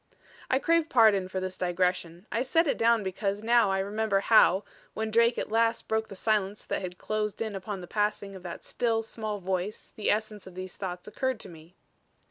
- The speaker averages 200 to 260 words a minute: Yes, fast, 205 wpm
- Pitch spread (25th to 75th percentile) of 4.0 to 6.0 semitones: No, average, 3.1 semitones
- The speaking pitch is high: Yes, high, 210 Hz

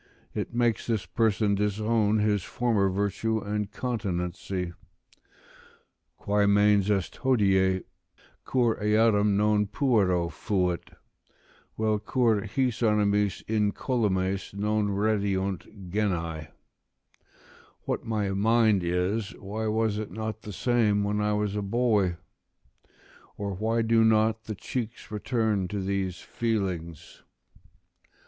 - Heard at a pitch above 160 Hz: No, low, 105 Hz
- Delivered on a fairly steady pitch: Yes, narrow, 2.2 semitones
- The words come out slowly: Yes, slow, 110 wpm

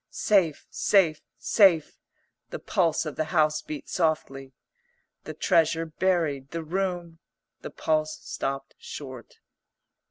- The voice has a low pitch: No, medium, 160 Hz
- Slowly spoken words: Yes, slow, 120 wpm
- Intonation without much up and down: Yes, narrow, 2.3 semitones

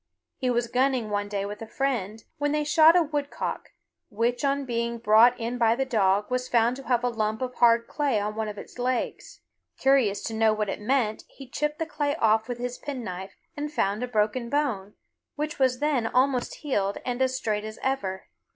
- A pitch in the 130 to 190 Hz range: No, high, 240 Hz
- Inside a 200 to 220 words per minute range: Yes, fast, 205 wpm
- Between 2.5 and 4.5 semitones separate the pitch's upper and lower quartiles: Yes, average, 3.8 semitones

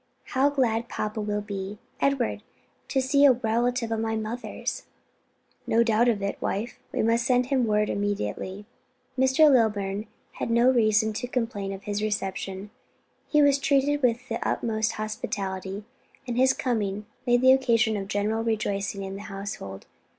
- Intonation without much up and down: No, average, 3.4 semitones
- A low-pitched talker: No, high, 220 Hz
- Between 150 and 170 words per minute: Yes, average, 160 wpm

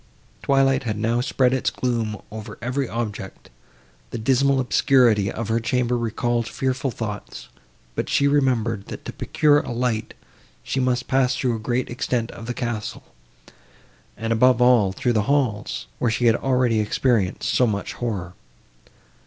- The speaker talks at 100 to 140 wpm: No, average, 155 wpm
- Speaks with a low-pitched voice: Yes, low, 120 Hz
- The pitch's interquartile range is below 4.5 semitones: Yes, narrow, 2.5 semitones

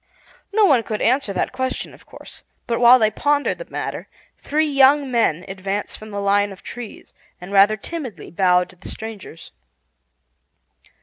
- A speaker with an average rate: Yes, average, 165 wpm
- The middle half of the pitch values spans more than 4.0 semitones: Yes, average, 5.2 semitones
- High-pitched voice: Yes, high, 220 Hz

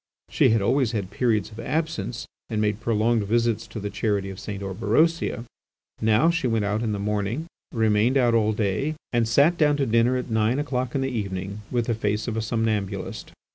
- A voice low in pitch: Yes, low, 115 Hz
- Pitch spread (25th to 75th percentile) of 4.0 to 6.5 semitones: No, average, 3.0 semitones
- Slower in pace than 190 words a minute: No, average, 200 wpm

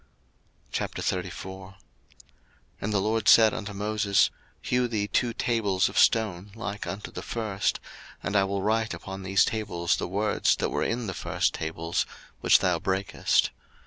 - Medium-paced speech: Yes, average, 150 wpm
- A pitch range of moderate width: No, narrow, 2.3 semitones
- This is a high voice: No, low, 100 Hz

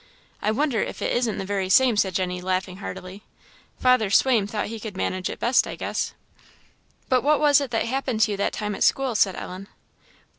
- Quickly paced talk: Yes, fast, 210 wpm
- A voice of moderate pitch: No, high, 215 Hz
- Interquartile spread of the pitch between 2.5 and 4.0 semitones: No, average, 4.9 semitones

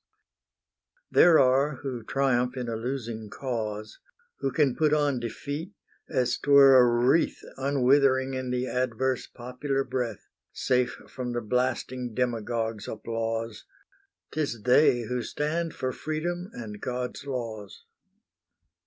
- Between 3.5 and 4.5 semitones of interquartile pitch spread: No, average, 2.7 semitones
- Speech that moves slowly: Yes, slow, 125 wpm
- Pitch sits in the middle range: No, low, 125 Hz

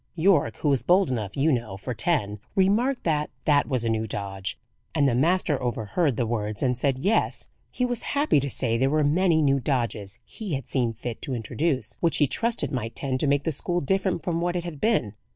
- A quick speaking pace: Yes, fast, 220 wpm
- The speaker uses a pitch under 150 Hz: Yes, medium, 140 Hz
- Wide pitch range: Yes, wide, 6.5 semitones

